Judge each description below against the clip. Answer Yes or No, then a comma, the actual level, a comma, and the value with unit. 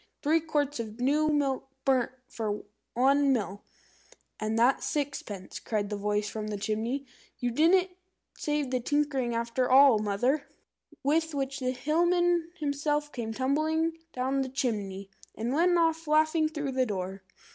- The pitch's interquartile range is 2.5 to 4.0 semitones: No, average, 5.0 semitones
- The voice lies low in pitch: No, very high, 270 Hz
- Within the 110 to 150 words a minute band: Yes, average, 145 wpm